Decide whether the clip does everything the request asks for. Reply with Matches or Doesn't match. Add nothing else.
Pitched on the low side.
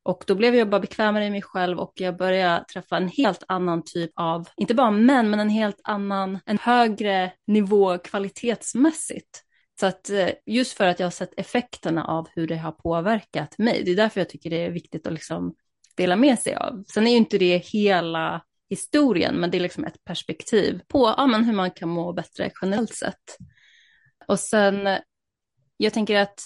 Doesn't match